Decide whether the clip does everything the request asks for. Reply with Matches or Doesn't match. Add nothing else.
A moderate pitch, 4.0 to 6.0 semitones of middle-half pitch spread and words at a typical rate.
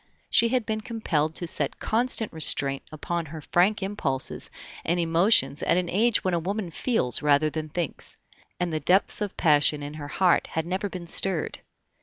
Matches